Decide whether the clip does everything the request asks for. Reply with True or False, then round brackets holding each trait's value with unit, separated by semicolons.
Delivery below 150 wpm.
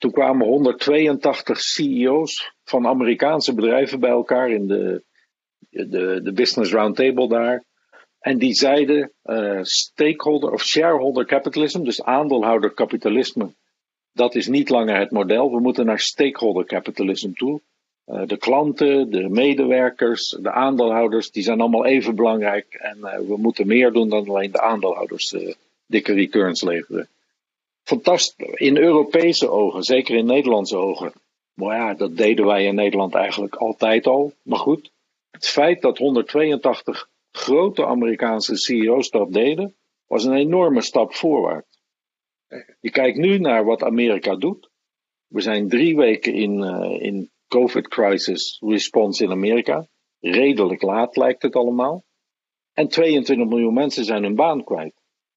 True (140 wpm)